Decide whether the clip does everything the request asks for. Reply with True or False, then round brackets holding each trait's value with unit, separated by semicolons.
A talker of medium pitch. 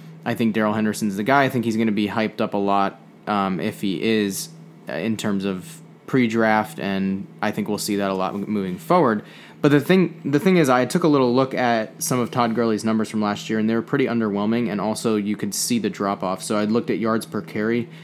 False (110 Hz)